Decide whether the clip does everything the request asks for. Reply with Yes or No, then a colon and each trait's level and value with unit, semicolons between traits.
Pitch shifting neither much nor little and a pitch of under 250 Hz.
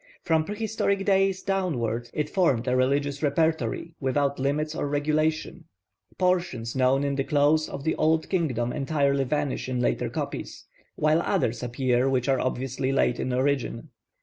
Yes: average, 3.5 semitones; medium, 140 Hz